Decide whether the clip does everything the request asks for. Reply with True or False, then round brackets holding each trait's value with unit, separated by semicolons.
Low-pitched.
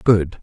True (95 Hz)